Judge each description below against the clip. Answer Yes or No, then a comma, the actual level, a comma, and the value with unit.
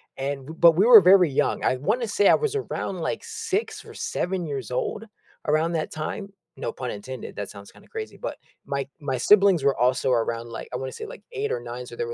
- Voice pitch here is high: No, medium, 150 Hz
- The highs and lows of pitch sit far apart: Yes, wide, 8.3 semitones